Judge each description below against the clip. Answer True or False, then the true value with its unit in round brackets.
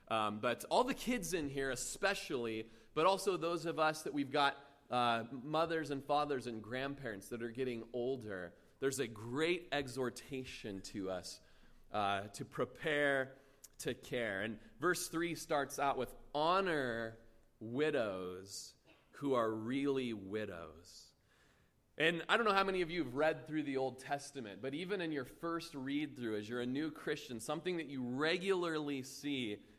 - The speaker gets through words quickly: False (160 wpm)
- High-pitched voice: False (135 Hz)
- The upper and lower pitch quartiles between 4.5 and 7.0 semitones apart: True (5.4 semitones)